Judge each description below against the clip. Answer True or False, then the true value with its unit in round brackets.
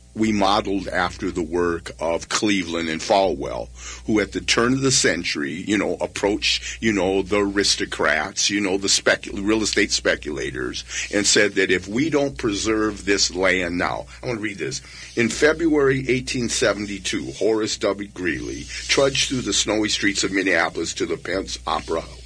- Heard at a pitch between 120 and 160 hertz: False (100 Hz)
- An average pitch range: True (3.6 semitones)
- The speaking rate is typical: True (170 wpm)